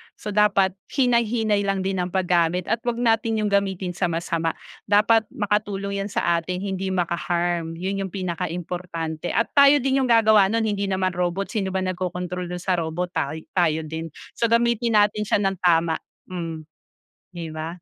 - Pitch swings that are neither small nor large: Yes, average, 3.4 semitones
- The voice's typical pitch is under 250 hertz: Yes, high, 190 Hz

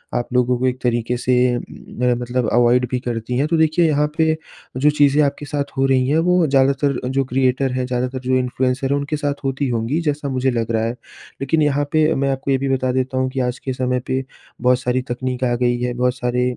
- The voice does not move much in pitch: Yes, narrow, 2.1 semitones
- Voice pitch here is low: Yes, low, 130 Hz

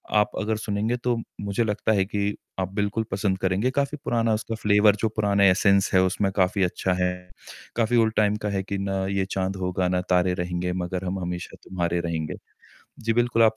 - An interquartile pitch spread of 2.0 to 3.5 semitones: Yes, average, 2.7 semitones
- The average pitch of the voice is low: Yes, low, 100 Hz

